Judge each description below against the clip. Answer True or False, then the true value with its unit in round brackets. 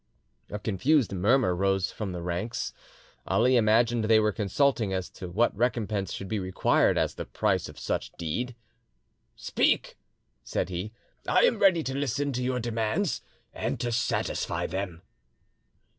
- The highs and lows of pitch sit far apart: False (4.5 semitones)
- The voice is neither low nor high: False (110 Hz)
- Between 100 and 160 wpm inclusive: True (150 wpm)